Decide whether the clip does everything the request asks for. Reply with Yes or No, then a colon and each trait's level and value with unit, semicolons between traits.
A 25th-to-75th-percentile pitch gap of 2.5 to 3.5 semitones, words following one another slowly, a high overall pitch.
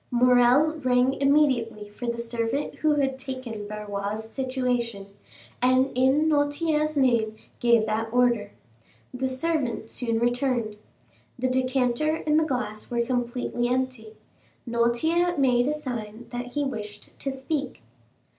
Yes: average, 2.9 semitones; slow, 125 wpm; very high, 250 Hz